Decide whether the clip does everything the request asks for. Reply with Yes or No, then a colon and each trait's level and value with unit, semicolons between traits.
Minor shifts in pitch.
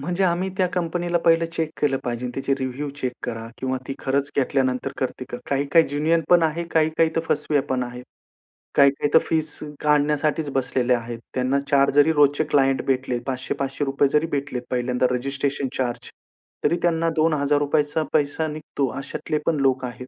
No: average, 3.1 semitones